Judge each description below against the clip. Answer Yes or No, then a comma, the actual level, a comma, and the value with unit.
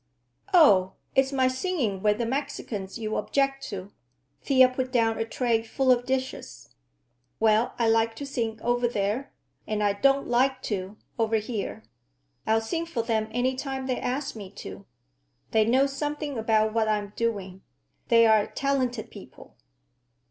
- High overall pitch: Yes, high, 230 Hz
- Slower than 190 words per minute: Yes, average, 155 wpm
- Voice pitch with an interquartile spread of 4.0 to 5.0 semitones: No, average, 3.4 semitones